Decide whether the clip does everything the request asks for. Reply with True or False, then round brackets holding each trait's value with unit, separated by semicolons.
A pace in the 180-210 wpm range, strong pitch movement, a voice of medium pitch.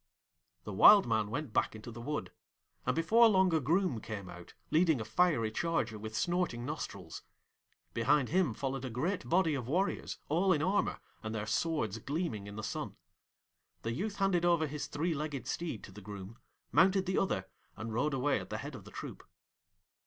True (190 wpm; 7.8 semitones; 145 Hz)